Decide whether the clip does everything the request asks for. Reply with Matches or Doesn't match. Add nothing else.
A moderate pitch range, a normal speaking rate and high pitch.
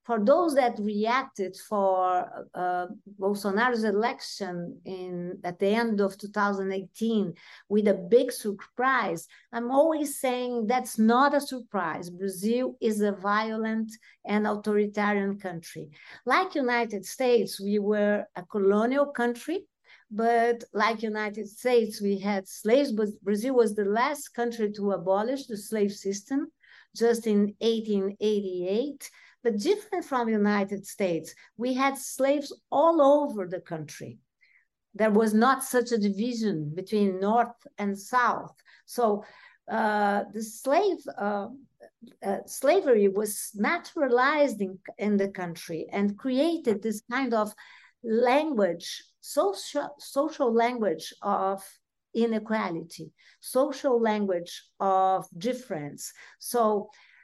Doesn't match